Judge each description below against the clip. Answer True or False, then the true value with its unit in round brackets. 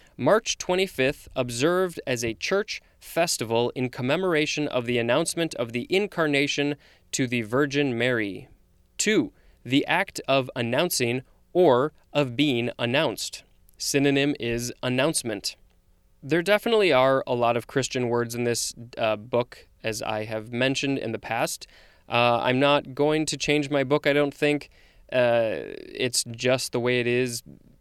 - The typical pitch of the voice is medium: False (125 Hz)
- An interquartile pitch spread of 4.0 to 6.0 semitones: False (3.5 semitones)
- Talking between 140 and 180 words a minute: True (145 wpm)